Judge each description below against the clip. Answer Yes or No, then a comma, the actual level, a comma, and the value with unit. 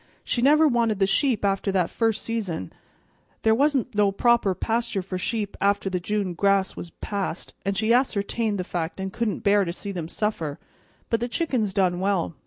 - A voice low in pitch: No, high, 200 Hz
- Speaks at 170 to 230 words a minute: Yes, average, 190 wpm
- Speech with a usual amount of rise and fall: Yes, average, 3.3 semitones